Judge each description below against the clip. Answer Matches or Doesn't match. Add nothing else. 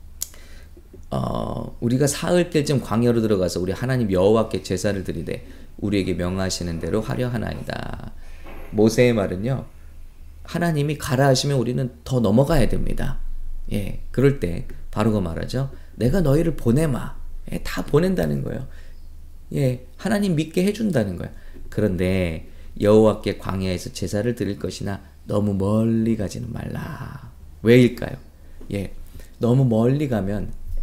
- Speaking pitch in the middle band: Doesn't match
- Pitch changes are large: Matches